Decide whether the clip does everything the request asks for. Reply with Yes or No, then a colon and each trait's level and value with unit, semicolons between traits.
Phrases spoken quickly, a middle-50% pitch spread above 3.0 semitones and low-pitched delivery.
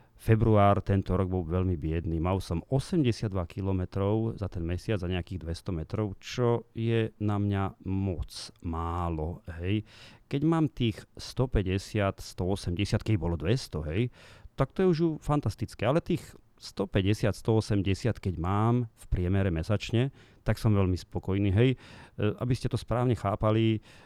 No: average, 145 wpm; average, 3.6 semitones; low, 105 Hz